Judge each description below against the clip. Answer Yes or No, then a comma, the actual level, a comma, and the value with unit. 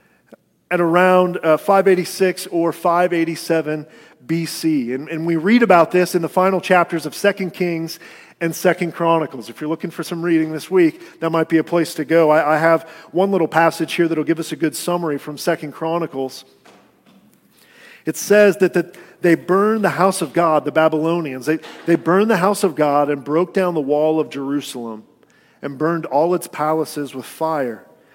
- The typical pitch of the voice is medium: Yes, medium, 165 Hz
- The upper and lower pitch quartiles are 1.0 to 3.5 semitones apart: Yes, narrow, 2.4 semitones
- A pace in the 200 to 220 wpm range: No, average, 185 wpm